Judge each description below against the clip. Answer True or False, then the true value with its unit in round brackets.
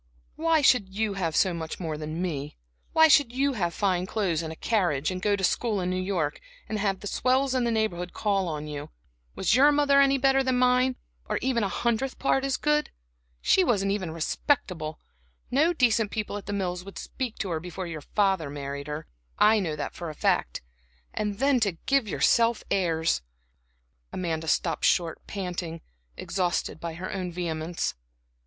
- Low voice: False (195 Hz)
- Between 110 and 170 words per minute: False (185 wpm)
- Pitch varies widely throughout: True (6.5 semitones)